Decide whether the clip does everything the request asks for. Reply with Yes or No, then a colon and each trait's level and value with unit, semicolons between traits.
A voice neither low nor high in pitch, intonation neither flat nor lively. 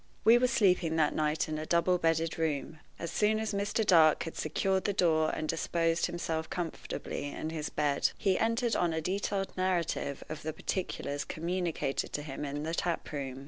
Yes: medium, 165 Hz; average, 3.2 semitones